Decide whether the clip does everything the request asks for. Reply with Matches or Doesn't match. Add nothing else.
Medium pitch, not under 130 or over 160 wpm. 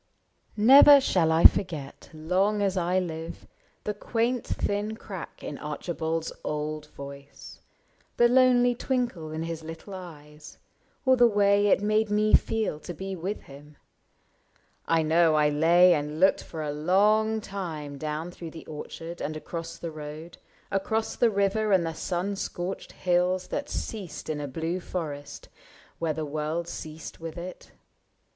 Matches